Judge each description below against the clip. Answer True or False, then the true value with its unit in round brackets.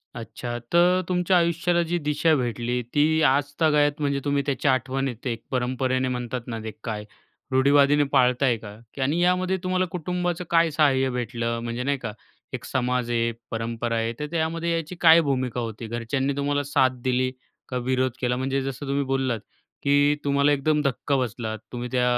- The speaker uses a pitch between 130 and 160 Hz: True (135 Hz)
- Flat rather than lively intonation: False (3.4 semitones)